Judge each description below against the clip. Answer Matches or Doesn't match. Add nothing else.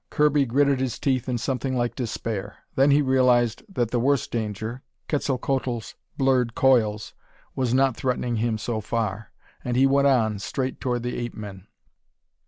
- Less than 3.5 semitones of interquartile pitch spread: Matches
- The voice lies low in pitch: Matches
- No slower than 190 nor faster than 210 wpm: Doesn't match